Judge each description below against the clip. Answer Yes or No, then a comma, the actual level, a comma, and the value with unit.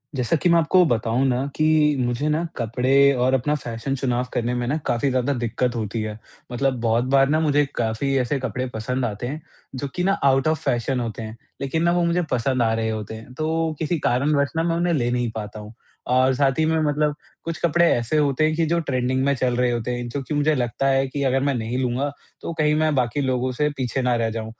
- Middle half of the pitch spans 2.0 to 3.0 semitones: No, average, 3.7 semitones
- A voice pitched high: No, low, 130 Hz